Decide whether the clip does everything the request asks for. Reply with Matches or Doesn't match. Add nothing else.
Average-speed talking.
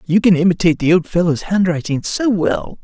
Matches